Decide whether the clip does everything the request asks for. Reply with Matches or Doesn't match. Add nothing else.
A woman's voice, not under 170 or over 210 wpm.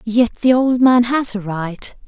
Matches